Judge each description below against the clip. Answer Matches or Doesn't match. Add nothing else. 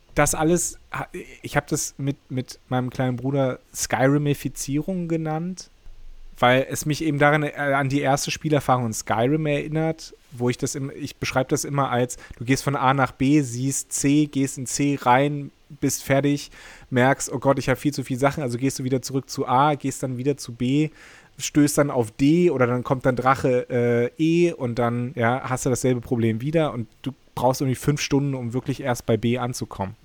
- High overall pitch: Doesn't match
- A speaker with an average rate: Doesn't match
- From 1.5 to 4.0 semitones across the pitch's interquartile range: Matches